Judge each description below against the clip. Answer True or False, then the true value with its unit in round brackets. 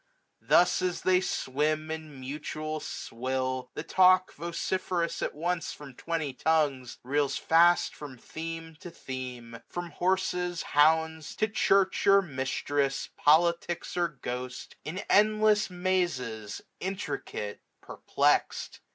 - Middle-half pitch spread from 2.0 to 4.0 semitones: False (4.9 semitones)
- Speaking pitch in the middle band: True (160 Hz)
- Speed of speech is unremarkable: False (115 wpm)